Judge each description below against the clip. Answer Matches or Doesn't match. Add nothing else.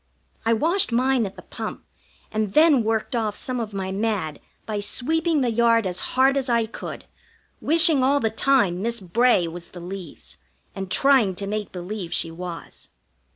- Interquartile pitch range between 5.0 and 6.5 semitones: Matches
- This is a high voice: Matches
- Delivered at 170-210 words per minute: Matches